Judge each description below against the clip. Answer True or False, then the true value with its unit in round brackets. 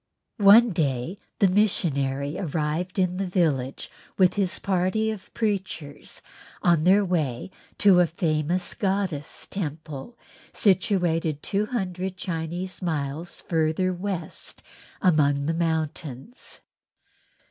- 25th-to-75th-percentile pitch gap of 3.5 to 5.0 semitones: True (3.8 semitones)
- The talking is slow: True (105 wpm)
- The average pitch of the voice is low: False (175 Hz)